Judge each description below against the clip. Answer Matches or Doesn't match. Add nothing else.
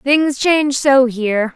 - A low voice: Doesn't match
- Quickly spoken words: Doesn't match